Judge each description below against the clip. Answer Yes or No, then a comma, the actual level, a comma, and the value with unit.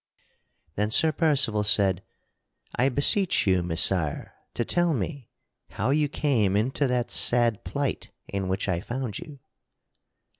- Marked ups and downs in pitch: Yes, wide, 6.3 semitones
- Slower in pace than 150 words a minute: Yes, slow, 135 wpm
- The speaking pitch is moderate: No, low, 120 Hz